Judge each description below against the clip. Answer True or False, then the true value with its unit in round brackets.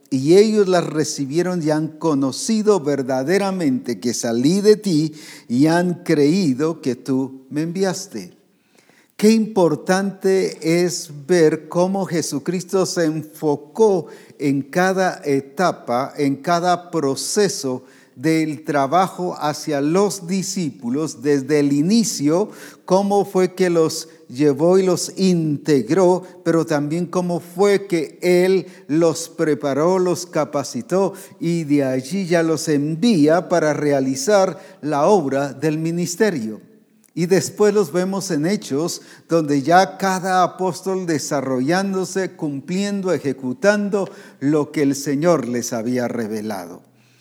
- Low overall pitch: False (165 Hz)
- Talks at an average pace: False (115 wpm)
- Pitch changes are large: False (4.4 semitones)